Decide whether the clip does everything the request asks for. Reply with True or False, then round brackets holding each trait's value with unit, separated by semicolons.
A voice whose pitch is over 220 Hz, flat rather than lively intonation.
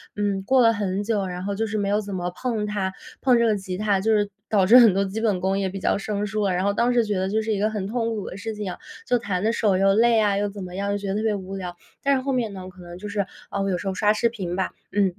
False (205 Hz; 2.3 semitones)